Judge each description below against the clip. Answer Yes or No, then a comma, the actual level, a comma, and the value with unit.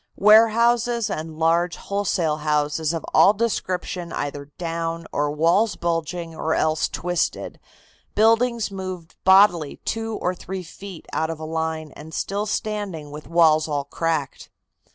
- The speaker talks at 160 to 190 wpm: No, slow, 135 wpm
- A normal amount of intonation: Yes, average, 4.2 semitones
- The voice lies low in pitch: No, medium, 170 Hz